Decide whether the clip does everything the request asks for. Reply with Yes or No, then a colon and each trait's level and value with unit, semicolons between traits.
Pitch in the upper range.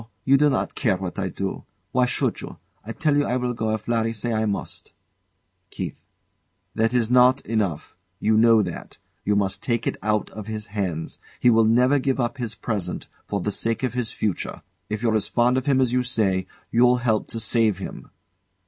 No: low, 115 Hz